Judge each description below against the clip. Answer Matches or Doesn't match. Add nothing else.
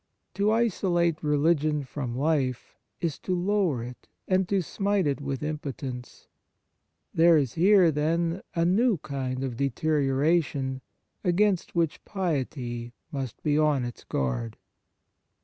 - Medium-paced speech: Doesn't match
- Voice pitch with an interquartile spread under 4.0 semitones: Doesn't match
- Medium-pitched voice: Matches